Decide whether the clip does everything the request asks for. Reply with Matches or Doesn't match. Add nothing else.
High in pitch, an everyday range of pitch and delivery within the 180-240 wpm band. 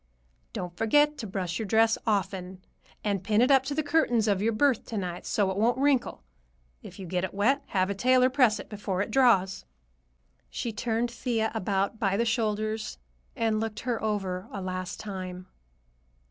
Matches